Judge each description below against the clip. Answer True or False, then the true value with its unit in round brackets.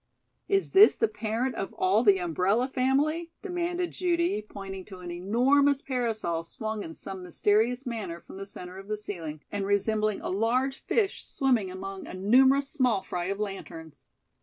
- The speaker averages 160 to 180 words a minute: True (165 wpm)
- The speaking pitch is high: True (215 Hz)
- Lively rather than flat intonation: True (5.8 semitones)